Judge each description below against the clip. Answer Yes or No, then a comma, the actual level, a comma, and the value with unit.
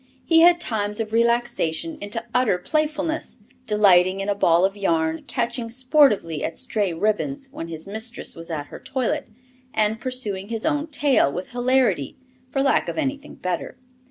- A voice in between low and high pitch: No, high, 225 Hz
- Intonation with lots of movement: Yes, wide, 6.1 semitones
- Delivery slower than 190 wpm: Yes, average, 160 wpm